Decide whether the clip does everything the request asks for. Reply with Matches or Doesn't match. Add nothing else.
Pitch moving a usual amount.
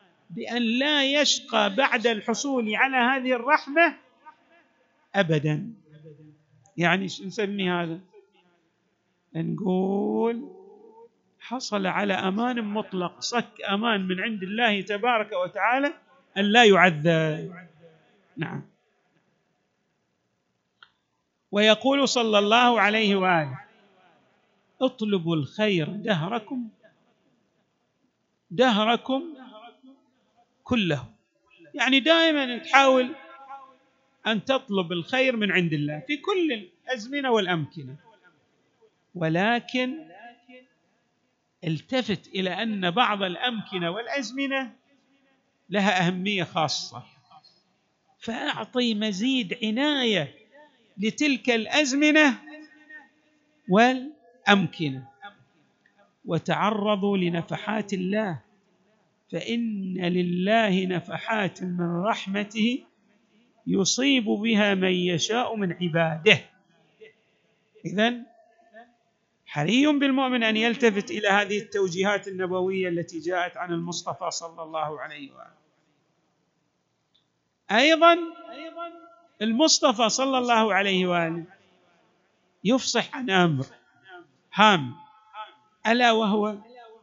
Doesn't match